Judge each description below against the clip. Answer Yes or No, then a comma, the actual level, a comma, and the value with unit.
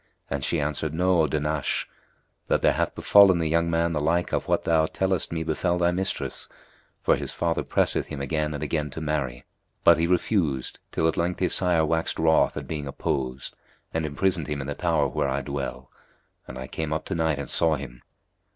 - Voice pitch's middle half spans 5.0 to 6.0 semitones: No, average, 2.8 semitones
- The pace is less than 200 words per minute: No, fast, 205 wpm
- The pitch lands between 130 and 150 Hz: No, very low, 80 Hz